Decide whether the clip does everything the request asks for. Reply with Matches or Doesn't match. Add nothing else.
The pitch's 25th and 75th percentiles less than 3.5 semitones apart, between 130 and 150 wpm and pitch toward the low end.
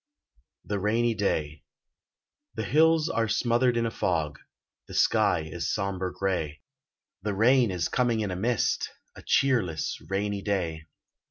Doesn't match